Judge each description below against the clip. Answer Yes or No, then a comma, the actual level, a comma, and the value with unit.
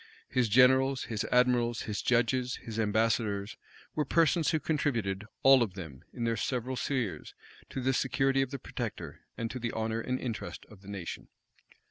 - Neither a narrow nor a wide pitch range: Yes, average, 3.1 semitones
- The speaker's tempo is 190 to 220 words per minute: No, average, 170 wpm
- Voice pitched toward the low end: Yes, low, 120 Hz